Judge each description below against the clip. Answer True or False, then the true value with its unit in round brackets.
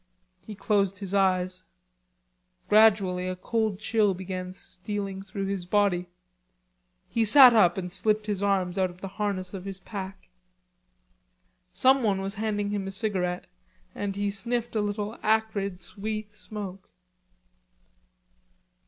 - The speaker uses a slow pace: True (130 wpm)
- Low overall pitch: False (200 Hz)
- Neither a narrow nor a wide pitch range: False (2.2 semitones)